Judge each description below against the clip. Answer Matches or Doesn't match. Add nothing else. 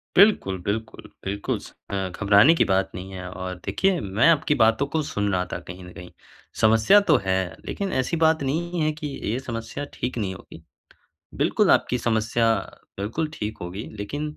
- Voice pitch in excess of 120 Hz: Doesn't match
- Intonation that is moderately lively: Doesn't match